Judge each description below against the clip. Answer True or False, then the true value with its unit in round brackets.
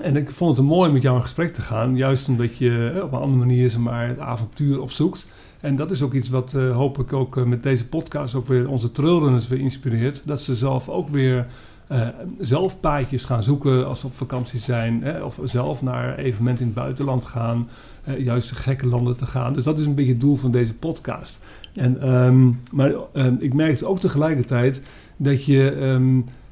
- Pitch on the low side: True (130 Hz)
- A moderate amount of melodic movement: False (2.1 semitones)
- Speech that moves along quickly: True (215 wpm)